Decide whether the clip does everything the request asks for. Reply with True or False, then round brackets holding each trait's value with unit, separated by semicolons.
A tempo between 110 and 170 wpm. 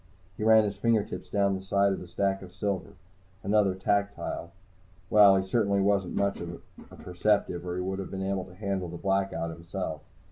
False (190 wpm)